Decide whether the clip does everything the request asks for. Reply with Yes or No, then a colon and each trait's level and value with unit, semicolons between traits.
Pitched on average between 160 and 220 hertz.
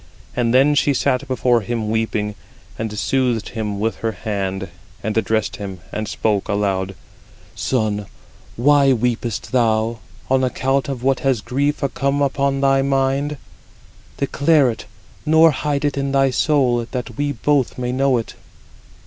No: low, 125 Hz